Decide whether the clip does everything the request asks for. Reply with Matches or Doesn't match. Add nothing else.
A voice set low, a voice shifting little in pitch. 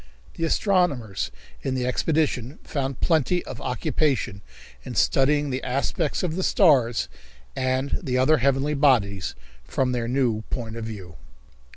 Doesn't match